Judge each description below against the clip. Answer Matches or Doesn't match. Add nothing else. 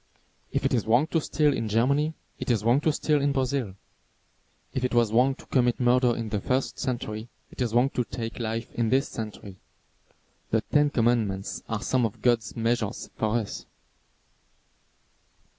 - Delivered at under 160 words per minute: Doesn't match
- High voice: Doesn't match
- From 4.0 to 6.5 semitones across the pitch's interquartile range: Doesn't match